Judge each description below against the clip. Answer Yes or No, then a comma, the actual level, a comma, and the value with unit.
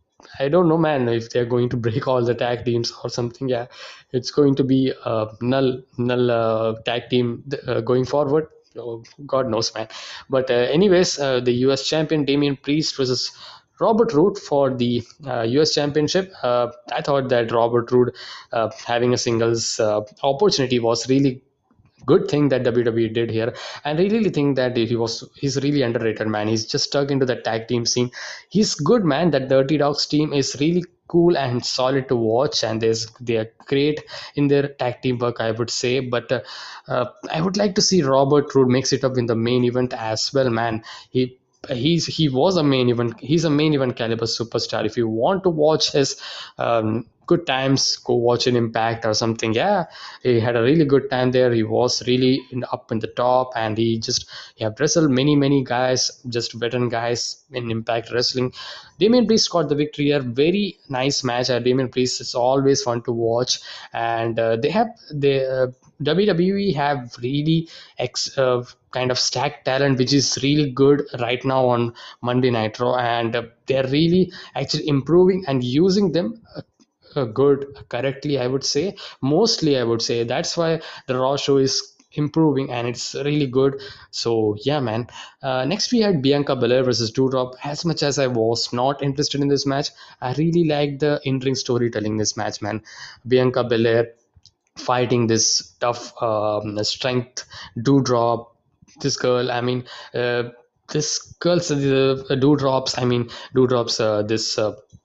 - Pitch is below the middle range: Yes, low, 130 Hz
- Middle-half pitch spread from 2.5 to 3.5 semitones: Yes, average, 3.2 semitones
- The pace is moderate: Yes, average, 180 wpm